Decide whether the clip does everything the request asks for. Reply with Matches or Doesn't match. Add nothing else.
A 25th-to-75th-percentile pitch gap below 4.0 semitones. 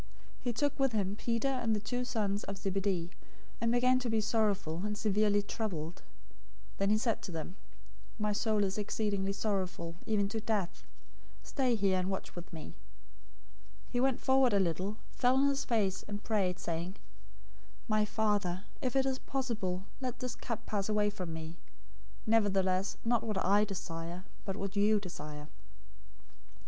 Matches